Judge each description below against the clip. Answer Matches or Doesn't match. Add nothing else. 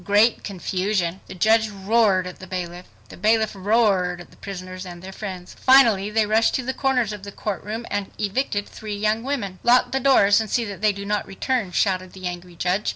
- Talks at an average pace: Doesn't match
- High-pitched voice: Matches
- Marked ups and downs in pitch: Doesn't match